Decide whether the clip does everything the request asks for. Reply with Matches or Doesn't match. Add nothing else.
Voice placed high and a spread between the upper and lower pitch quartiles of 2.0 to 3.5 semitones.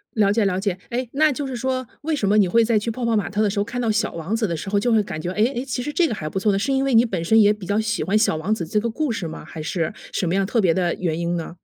Doesn't match